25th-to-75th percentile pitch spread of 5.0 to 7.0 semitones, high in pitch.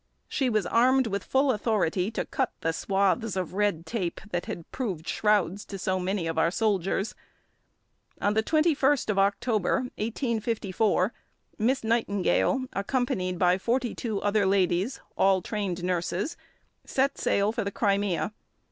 No: average, 3.9 semitones; high, 205 Hz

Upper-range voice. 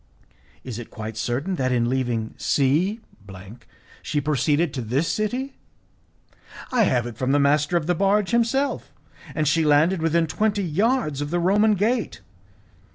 No: medium, 155 Hz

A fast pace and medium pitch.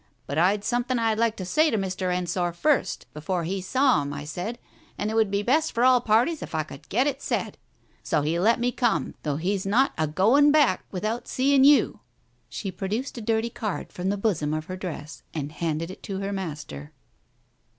No: fast, 215 wpm; high, 195 Hz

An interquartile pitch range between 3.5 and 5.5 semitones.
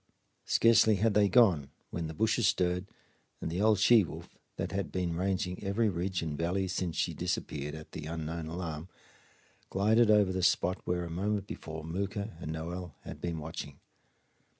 Yes: average, 3.8 semitones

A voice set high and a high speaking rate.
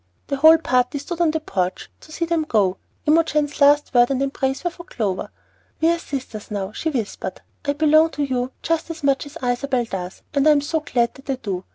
Yes: very high, 280 Hz; fast, 220 wpm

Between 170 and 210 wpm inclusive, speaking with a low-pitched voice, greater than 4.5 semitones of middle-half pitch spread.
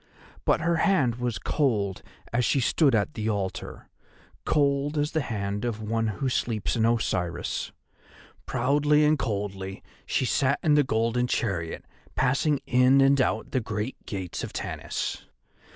No: average, 150 wpm; low, 120 Hz; average, 4.9 semitones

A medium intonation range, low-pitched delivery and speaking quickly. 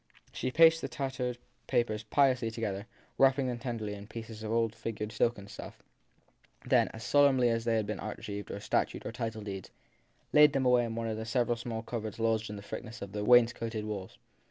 No: narrow, 2.3 semitones; low, 115 Hz; fast, 210 wpm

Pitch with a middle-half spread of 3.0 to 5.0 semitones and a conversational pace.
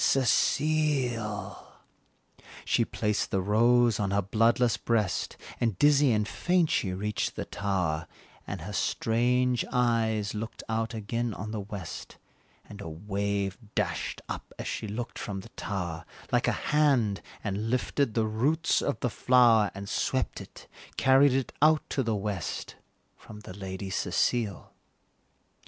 Yes: average, 3.5 semitones; average, 145 wpm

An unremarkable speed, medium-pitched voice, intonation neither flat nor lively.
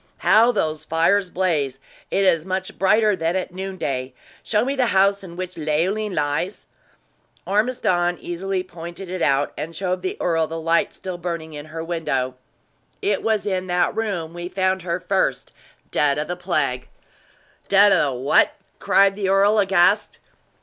Yes: average, 165 wpm; medium, 180 Hz; average, 3.2 semitones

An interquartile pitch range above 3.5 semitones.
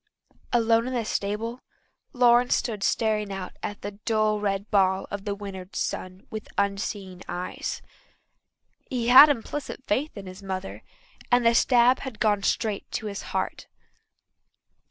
No: average, 3.2 semitones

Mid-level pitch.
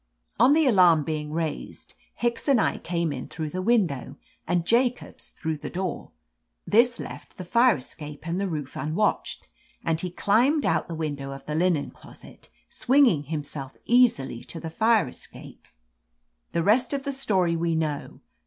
Yes: medium, 170 Hz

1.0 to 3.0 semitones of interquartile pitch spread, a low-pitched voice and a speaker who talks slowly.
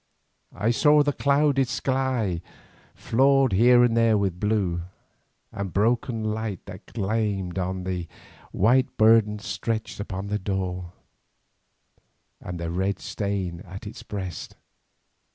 No: average, 3.8 semitones; low, 105 Hz; slow, 125 wpm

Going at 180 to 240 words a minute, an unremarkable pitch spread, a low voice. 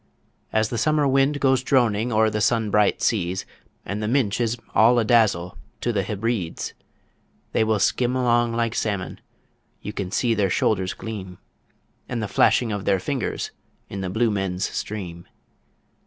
No: average, 165 wpm; average, 3.4 semitones; low, 110 Hz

